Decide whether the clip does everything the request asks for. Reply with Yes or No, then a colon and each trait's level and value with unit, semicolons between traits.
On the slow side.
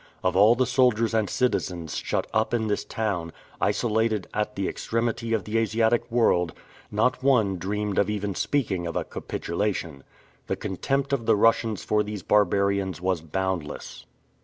No: average, 160 wpm